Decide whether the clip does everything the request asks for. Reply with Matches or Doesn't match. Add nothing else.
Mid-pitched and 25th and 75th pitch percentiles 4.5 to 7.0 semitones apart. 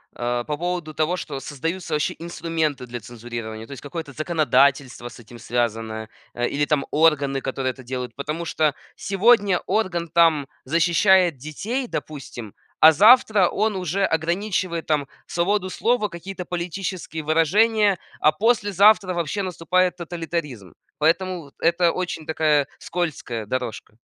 Matches